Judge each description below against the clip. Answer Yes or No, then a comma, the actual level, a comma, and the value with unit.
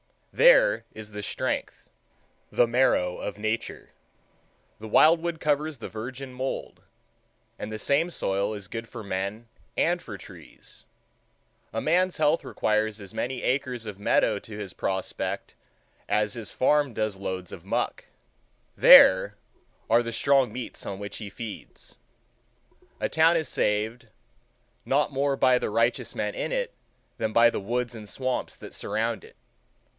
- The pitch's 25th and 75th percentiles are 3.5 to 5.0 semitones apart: Yes, average, 4.7 semitones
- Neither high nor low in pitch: No, low, 115 Hz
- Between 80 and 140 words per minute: No, average, 150 wpm